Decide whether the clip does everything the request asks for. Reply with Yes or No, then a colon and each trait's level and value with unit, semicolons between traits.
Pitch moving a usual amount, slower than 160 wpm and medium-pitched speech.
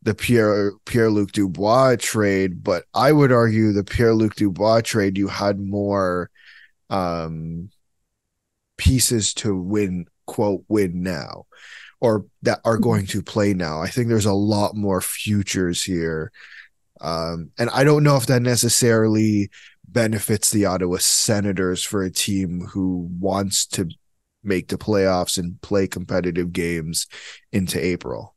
No: average, 3.2 semitones; average, 140 wpm; low, 100 Hz